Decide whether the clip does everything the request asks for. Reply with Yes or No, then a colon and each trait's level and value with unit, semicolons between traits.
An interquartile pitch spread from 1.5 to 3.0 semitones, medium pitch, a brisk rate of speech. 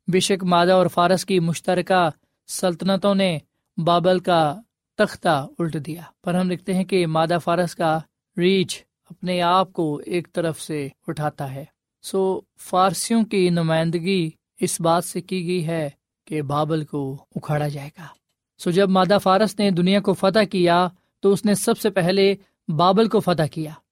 No: average, 2.7 semitones; medium, 180 Hz; average, 170 wpm